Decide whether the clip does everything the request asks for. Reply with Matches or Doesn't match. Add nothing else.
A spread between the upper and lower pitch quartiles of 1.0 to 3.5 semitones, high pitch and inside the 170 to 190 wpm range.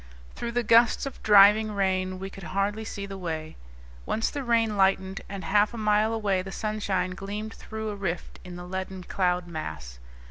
Matches